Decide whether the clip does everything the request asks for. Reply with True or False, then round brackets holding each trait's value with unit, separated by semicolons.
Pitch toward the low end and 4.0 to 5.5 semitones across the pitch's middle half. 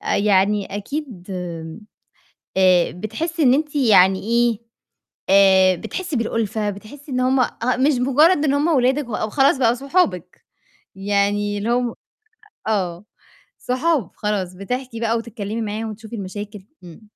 False (220 Hz; 4.7 semitones)